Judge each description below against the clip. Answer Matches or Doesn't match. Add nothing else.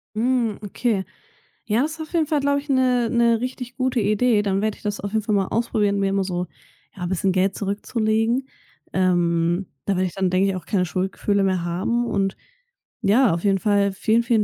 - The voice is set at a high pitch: Matches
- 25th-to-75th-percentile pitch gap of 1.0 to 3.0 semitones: Doesn't match